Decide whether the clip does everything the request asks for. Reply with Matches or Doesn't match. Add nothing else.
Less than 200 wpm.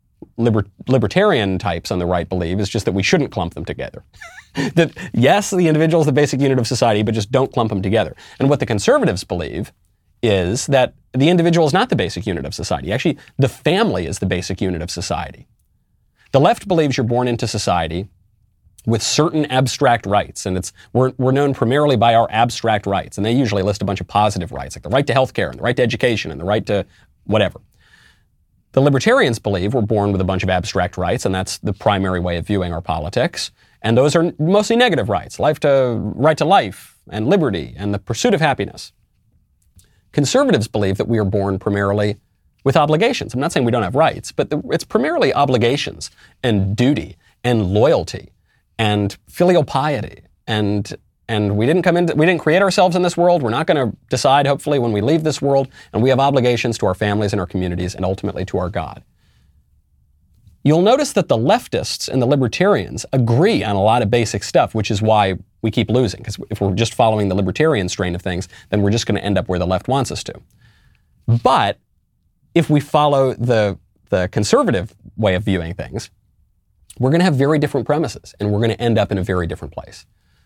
Doesn't match